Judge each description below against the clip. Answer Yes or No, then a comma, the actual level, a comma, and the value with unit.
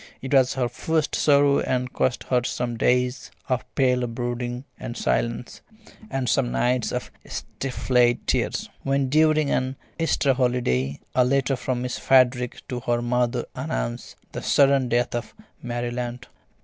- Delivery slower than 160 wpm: Yes, average, 150 wpm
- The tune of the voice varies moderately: No, narrow, 1.7 semitones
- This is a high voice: No, low, 125 Hz